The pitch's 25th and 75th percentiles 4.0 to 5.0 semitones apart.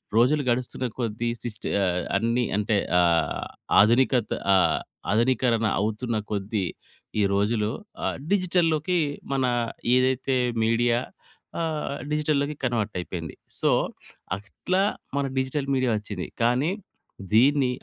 Yes: average, 4.4 semitones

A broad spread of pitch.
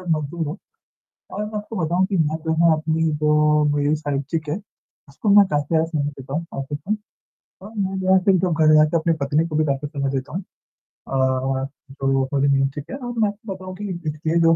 No: average, 4.2 semitones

